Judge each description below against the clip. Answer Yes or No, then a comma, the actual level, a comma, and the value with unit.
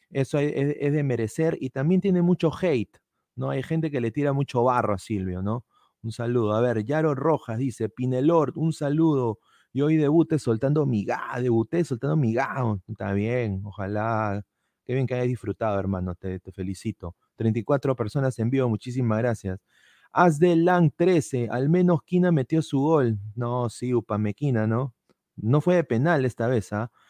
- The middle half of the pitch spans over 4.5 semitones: Yes, average, 5.0 semitones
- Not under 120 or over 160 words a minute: No, average, 175 wpm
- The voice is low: Yes, low, 125 Hz